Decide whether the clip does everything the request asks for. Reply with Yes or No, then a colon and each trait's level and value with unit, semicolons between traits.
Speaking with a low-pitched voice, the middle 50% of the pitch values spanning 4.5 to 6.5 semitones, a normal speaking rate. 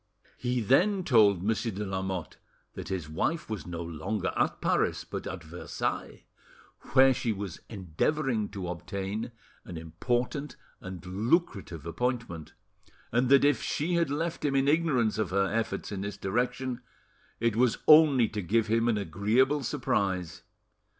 Yes: low, 110 Hz; wide, 5.6 semitones; average, 150 wpm